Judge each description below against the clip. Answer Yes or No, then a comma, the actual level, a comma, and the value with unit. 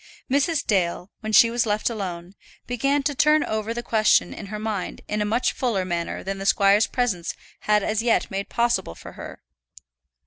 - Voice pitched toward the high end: Yes, high, 215 Hz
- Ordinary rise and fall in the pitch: Yes, average, 3.4 semitones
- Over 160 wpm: Yes, average, 185 wpm